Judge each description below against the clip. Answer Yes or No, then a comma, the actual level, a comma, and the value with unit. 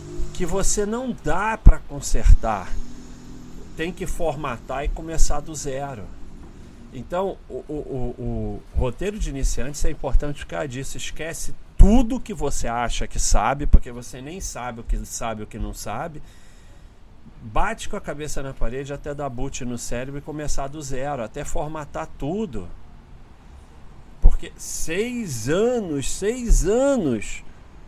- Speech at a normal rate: Yes, average, 140 wpm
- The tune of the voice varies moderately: No, wide, 6.6 semitones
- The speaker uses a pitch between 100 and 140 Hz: Yes, low, 135 Hz